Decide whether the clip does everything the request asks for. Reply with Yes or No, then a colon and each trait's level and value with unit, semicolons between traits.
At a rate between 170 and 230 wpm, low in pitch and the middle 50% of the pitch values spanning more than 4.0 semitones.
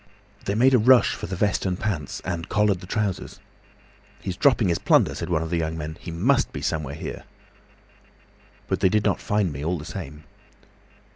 Yes: average, 200 wpm; very low, 90 Hz; average, 4.5 semitones